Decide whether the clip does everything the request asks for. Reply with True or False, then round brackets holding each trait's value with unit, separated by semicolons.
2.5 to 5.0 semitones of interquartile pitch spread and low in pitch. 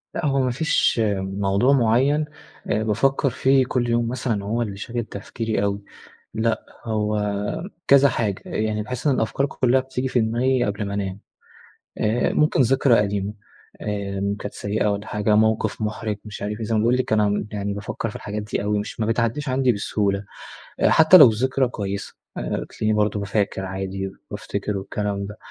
True (3.4 semitones; 110 Hz)